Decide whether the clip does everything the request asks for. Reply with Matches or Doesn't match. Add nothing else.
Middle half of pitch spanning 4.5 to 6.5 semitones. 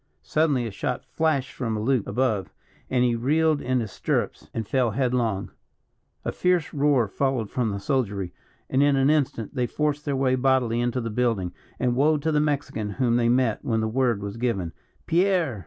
Doesn't match